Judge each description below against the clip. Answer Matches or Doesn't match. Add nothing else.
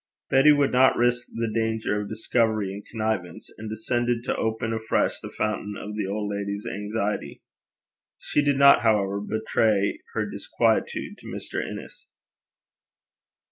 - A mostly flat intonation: Matches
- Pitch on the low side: Matches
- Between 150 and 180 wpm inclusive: Doesn't match